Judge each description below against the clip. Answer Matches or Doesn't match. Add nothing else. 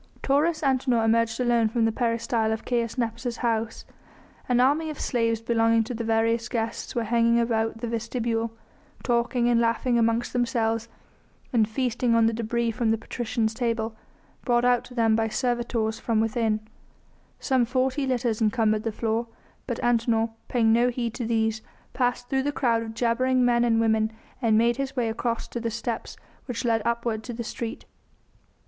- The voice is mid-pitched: Doesn't match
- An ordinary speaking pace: Matches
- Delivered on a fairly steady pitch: Matches